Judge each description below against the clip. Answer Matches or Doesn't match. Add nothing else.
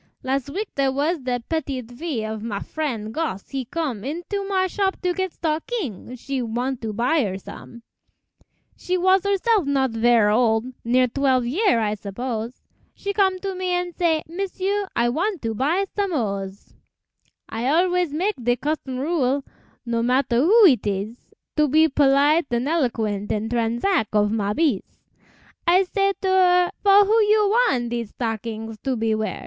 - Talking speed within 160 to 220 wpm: Matches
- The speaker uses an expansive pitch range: Matches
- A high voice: Matches